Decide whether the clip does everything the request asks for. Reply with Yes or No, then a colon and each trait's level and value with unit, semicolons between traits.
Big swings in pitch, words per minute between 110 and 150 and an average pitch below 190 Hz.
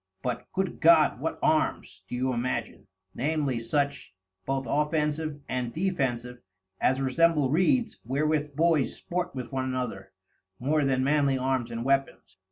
No: average, 3.2 semitones; average, 140 wpm; low, 135 Hz